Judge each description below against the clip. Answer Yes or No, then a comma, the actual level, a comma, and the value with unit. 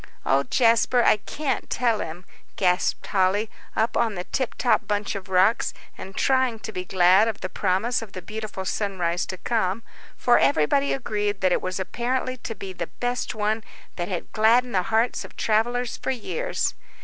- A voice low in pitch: No, high, 215 Hz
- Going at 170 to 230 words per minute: Yes, average, 175 wpm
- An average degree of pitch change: Yes, average, 4.2 semitones